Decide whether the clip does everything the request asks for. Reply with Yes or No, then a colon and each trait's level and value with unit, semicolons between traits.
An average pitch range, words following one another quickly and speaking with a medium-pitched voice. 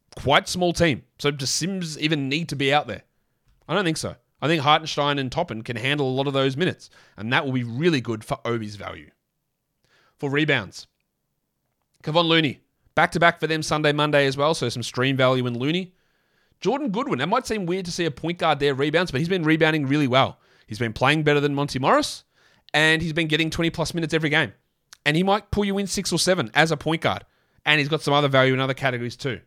Yes: average, 3.7 semitones; fast, 230 wpm; medium, 150 Hz